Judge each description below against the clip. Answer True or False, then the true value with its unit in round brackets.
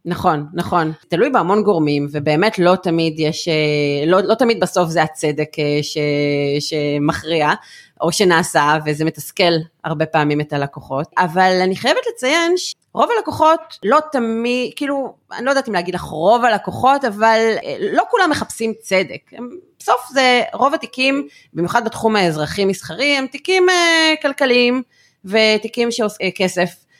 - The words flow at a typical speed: True (135 wpm)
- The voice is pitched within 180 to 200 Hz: True (190 Hz)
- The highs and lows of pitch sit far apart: True (8.3 semitones)